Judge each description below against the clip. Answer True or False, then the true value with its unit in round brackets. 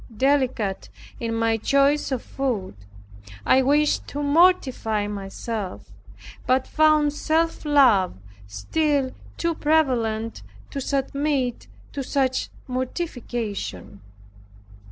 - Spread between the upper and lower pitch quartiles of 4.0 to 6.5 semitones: True (4.5 semitones)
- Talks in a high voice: True (260 Hz)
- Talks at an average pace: False (95 wpm)